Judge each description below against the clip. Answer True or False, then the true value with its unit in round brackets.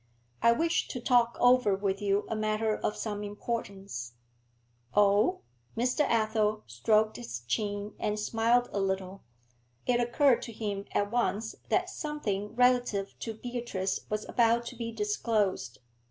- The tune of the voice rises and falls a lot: False (2.8 semitones)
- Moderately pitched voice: False (215 Hz)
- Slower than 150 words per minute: True (140 wpm)